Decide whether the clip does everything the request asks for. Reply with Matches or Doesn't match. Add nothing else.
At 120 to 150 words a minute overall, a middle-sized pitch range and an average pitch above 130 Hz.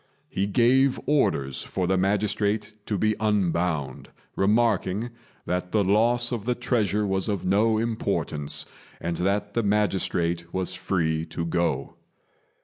Doesn't match